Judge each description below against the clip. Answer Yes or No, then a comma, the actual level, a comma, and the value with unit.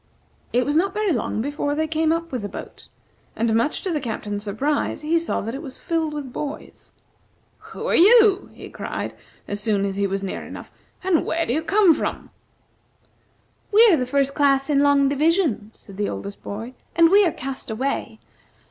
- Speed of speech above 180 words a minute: Yes, average, 195 wpm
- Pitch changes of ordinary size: No, wide, 6.4 semitones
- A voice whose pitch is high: Yes, very high, 285 Hz